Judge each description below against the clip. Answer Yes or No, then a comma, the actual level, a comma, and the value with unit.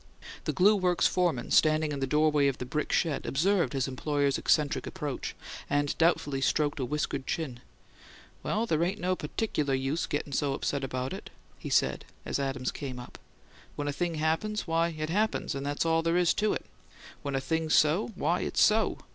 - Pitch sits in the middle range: Yes, medium, 150 Hz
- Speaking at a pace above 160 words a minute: Yes, average, 190 wpm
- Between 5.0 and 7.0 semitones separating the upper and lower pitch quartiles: No, average, 3.5 semitones